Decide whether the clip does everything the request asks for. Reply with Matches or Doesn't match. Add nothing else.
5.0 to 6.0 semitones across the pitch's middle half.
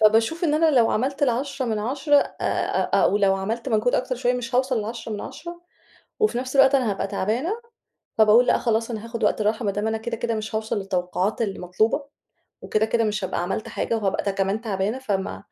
Doesn't match